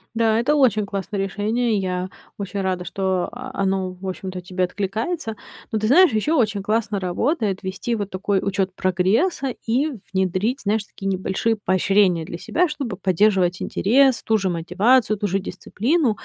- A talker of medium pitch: No, high, 200 Hz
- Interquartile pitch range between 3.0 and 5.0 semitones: Yes, average, 3.6 semitones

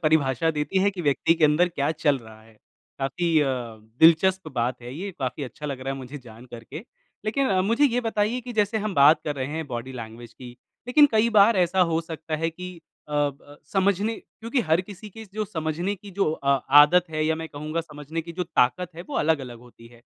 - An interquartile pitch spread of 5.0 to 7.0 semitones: Yes, wide, 5.4 semitones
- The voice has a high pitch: No, medium, 160 Hz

